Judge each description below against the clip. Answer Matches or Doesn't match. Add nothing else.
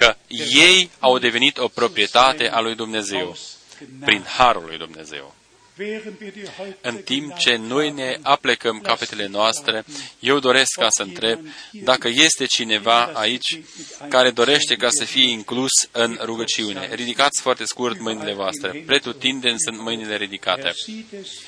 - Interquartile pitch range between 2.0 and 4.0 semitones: Matches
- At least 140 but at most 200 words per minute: Doesn't match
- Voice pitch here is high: Doesn't match